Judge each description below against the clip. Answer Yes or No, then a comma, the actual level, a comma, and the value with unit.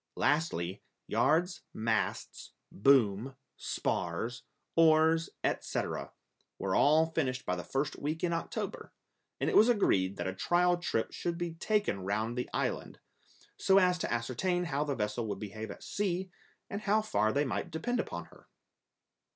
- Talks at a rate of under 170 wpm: Yes, average, 150 wpm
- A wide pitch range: Yes, wide, 8.2 semitones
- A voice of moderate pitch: Yes, medium, 145 Hz